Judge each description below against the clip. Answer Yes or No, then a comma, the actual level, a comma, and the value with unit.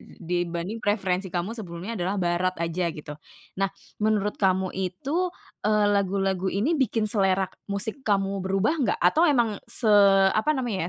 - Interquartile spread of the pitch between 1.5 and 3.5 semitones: Yes, average, 3.0 semitones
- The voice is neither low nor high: No, high, 195 Hz